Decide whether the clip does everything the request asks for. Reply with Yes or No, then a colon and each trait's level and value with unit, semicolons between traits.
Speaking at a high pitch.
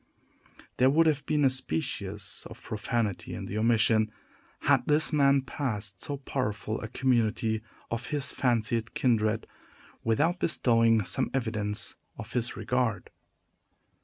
No: low, 115 Hz